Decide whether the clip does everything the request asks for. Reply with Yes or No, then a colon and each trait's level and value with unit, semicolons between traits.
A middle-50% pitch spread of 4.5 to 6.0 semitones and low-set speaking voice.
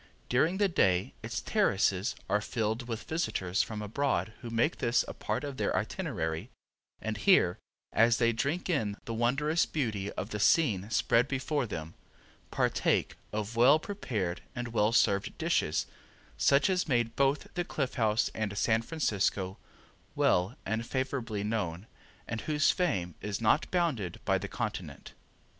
Yes: average, 5.2 semitones; low, 115 Hz